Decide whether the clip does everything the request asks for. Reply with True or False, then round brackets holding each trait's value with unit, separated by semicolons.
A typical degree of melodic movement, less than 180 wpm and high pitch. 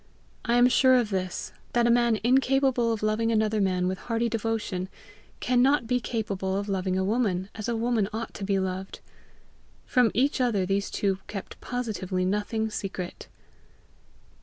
True (3.7 semitones; 165 wpm; 220 Hz)